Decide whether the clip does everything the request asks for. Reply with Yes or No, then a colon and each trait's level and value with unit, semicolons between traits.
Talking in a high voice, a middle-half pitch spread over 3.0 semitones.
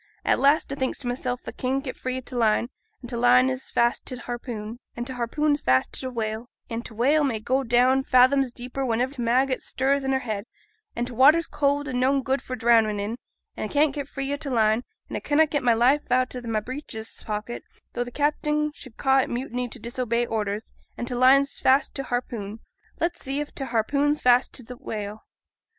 No: very high, 255 Hz; narrow, 2.5 semitones